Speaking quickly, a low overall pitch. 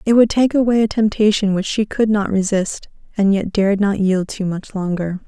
No: fast, 215 wpm; high, 205 Hz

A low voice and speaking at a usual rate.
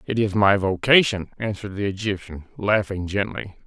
Yes: low, 100 Hz; average, 145 wpm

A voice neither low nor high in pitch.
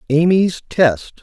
Yes: medium, 165 Hz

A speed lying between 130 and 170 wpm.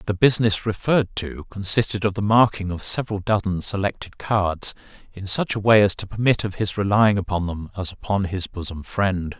No: average, 190 wpm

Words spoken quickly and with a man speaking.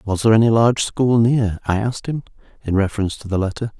Yes: fast, 220 wpm; male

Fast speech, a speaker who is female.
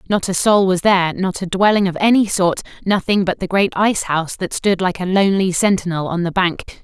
Yes: fast, 230 wpm; female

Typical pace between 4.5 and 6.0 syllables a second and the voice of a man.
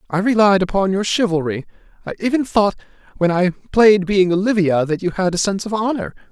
Yes: 5.8 syllables/s; male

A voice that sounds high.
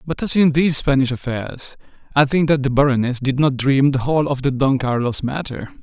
No: medium, 140 Hz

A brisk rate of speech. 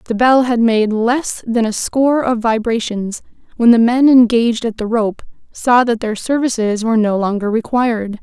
No: average, 180 wpm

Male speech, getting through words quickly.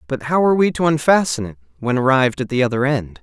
Yes: male; fast, 240 wpm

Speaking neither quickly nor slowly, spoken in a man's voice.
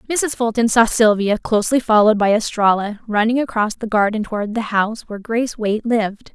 No: average, 180 wpm; female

